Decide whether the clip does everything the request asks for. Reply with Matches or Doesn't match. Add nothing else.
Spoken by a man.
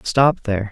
Matches